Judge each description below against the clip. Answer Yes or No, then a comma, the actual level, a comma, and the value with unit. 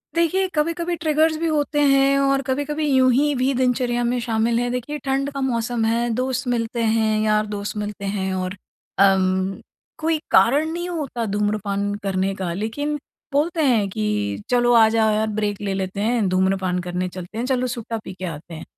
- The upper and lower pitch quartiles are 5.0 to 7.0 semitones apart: Yes, wide, 5.4 semitones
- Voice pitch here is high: Yes, high, 230 Hz